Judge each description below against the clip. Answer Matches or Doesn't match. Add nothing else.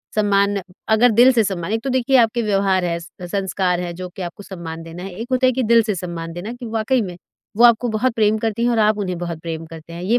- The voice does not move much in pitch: Doesn't match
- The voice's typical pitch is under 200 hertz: Doesn't match